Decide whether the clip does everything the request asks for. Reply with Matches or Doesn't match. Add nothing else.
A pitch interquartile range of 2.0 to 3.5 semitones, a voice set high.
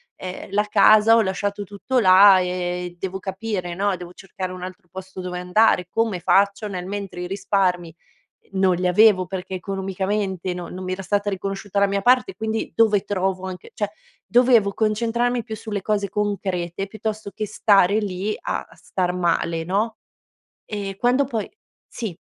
Matches